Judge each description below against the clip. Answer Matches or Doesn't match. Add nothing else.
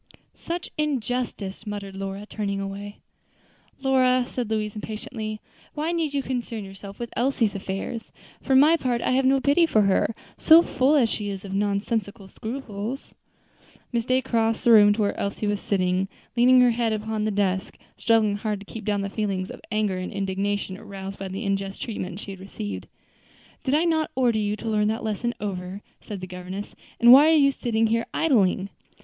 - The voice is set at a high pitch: Matches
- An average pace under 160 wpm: Doesn't match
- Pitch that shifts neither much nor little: Matches